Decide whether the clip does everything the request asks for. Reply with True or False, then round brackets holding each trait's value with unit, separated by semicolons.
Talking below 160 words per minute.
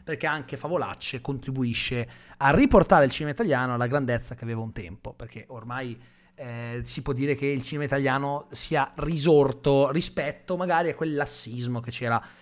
False (165 wpm)